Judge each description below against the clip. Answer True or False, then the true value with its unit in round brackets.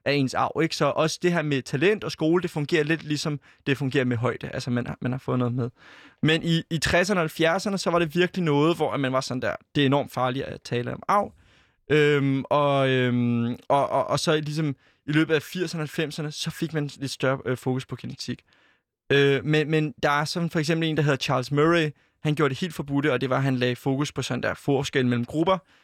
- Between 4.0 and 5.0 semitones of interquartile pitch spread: False (3.2 semitones)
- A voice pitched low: False (145 Hz)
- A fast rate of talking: True (245 wpm)